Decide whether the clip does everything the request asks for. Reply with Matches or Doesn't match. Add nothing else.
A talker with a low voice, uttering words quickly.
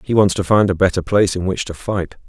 Matches